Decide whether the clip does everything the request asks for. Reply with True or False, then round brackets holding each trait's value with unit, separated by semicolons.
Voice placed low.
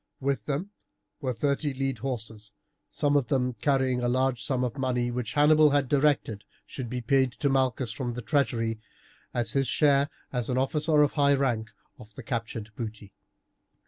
True (130 Hz)